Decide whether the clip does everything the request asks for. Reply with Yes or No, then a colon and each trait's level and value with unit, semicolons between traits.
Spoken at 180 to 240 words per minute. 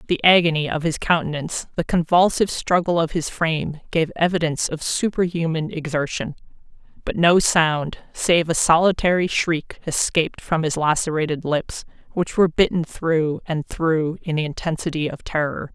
No: average, 150 wpm